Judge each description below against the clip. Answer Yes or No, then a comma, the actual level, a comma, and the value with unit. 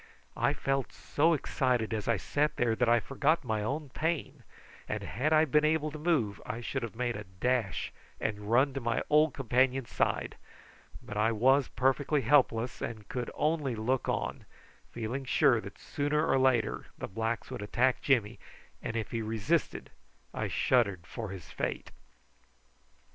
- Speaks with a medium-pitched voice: No, low, 125 Hz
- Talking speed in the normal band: Yes, average, 165 wpm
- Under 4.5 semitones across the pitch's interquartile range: Yes, average, 4.0 semitones